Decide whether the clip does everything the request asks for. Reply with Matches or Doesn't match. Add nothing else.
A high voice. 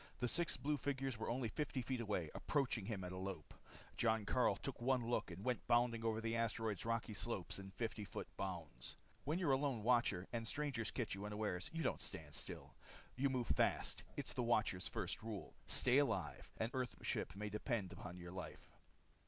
Doesn't match